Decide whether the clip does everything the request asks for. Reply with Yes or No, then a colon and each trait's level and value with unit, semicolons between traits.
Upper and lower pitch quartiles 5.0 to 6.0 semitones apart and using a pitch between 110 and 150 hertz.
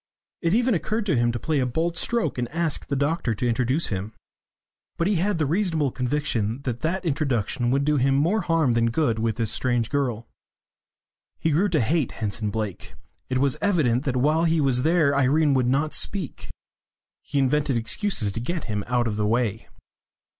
Yes: wide, 5.4 semitones; medium, 140 Hz